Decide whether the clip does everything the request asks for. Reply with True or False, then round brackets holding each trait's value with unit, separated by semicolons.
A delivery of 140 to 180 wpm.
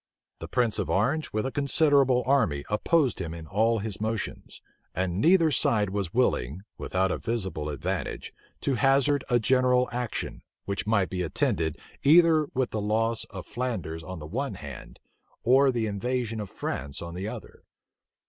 True (165 wpm)